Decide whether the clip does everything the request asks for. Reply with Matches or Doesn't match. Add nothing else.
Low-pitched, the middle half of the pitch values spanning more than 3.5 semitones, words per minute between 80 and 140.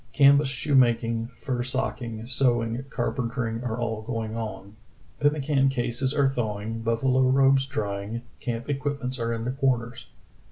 Doesn't match